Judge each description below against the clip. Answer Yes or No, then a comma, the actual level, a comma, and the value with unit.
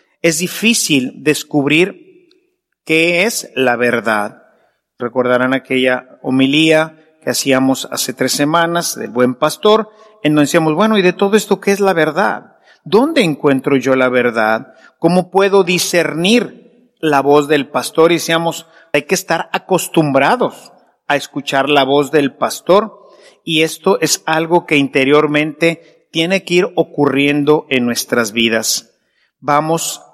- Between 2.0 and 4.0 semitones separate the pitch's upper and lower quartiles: No, average, 4.8 semitones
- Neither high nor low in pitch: Yes, medium, 155 Hz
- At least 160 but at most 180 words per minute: No, slow, 135 wpm